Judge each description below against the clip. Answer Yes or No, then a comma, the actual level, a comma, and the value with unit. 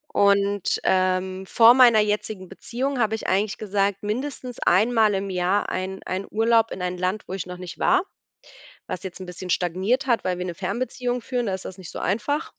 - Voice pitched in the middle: No, high, 200 Hz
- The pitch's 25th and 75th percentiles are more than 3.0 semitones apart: Yes, average, 3.7 semitones